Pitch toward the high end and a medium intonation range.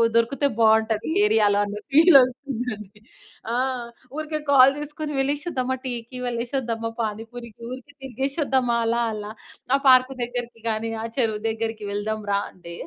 Yes: high, 240 Hz; average, 3.4 semitones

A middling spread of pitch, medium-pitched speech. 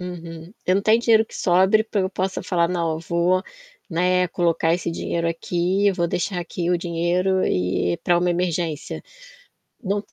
No: narrow, 1.8 semitones; medium, 175 Hz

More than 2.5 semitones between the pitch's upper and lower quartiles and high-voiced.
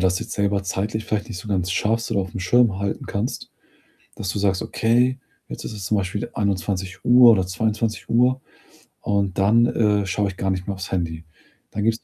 No: average, 2.9 semitones; low, 100 Hz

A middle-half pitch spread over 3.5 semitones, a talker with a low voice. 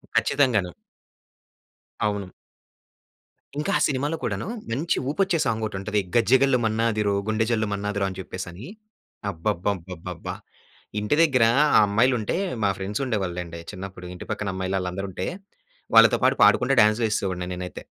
Yes: average, 3.9 semitones; low, 105 Hz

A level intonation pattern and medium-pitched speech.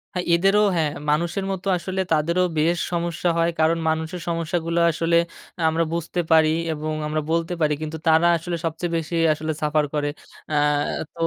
Yes: narrow, 1.6 semitones; medium, 165 Hz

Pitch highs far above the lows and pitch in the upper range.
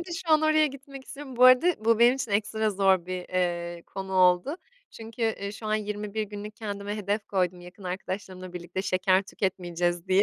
No: average, 3.8 semitones; high, 205 Hz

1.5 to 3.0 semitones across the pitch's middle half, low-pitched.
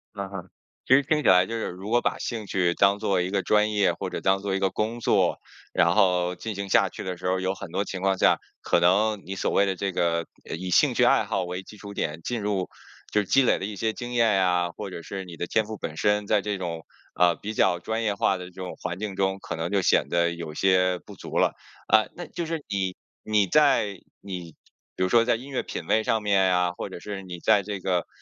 Yes: average, 2.7 semitones; very low, 95 Hz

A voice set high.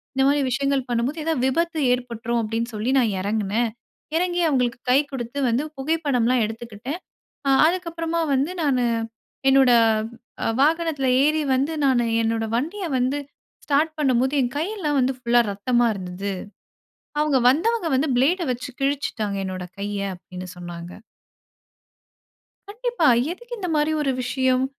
Yes: very high, 260 Hz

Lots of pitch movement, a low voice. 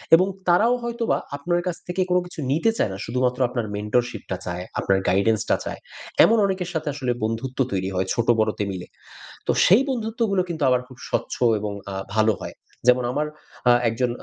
Yes: wide, 8.5 semitones; low, 130 Hz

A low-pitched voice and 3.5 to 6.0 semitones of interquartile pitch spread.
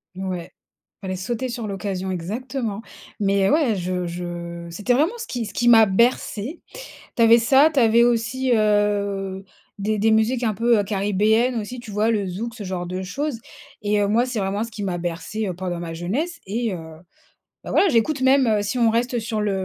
No: high, 215 Hz; average, 3.9 semitones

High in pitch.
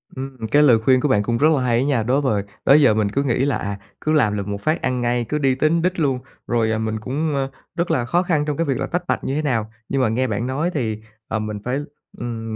No: low, 130 Hz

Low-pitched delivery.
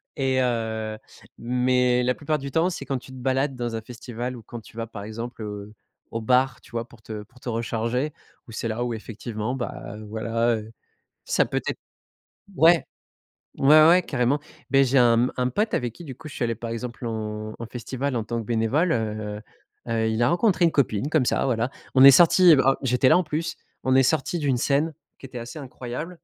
Yes: low, 125 Hz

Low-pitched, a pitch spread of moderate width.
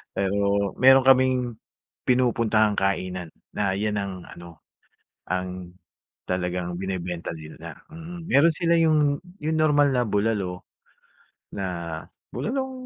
No: low, 100 Hz; wide, 7.3 semitones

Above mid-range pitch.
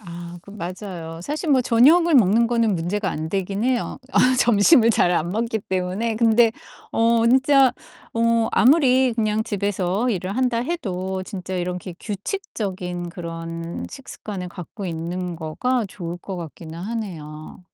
Yes: high, 200 Hz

